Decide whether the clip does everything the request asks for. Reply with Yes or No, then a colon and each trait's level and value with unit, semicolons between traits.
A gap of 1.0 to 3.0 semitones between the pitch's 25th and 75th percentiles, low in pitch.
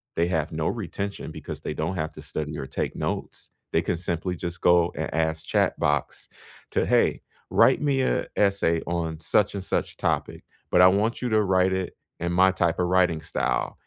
Yes: average, 2.7 semitones; very low, 90 Hz